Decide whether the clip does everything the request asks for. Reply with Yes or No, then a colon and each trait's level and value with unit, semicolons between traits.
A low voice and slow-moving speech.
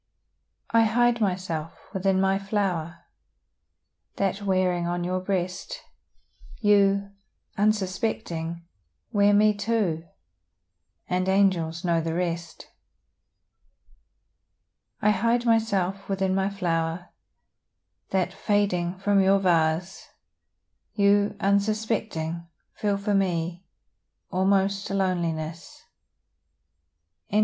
No: high, 190 Hz; slow, 90 wpm